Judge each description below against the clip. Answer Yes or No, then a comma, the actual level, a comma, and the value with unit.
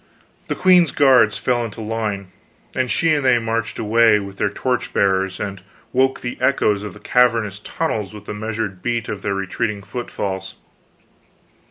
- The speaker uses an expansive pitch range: No, average, 3.4 semitones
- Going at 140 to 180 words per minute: Yes, average, 165 wpm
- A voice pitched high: No, low, 110 Hz